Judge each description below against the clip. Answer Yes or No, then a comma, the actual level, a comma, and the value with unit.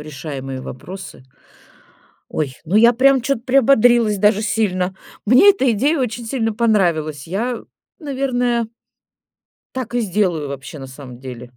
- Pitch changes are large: Yes, wide, 8.0 semitones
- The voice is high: Yes, high, 215 Hz